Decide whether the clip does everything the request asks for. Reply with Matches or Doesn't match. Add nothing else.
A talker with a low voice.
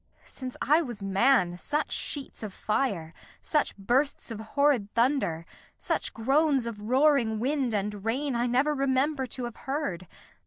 Doesn't match